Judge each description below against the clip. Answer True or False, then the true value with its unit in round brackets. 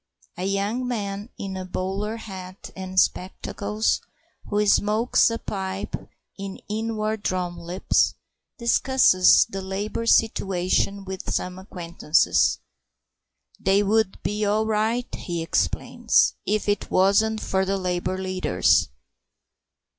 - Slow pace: True (115 wpm)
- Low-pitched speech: False (195 Hz)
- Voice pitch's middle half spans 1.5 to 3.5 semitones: True (2.4 semitones)